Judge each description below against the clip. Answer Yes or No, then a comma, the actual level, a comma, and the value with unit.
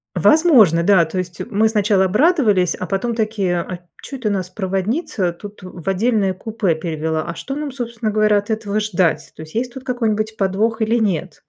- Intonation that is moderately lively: Yes, average, 3.7 semitones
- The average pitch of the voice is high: Yes, high, 205 Hz